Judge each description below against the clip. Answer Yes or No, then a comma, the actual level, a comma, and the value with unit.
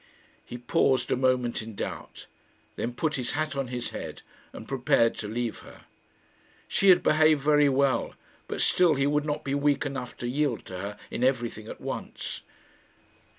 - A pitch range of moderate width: Yes, average, 3.4 semitones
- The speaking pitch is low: Yes, low, 130 Hz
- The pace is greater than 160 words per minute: Yes, average, 175 wpm